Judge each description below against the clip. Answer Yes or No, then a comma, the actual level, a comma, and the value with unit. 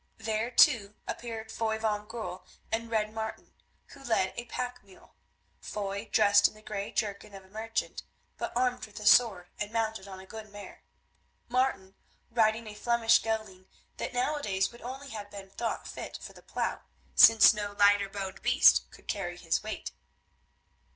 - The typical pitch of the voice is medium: No, high, 215 Hz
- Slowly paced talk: No, average, 170 wpm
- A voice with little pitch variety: Yes, narrow, 2.2 semitones